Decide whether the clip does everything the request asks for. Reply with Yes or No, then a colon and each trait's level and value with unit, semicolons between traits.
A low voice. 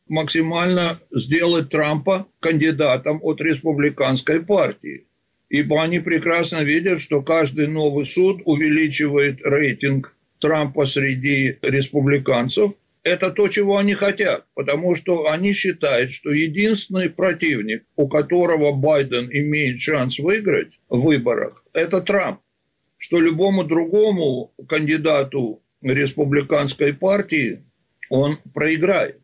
No: medium, 155 Hz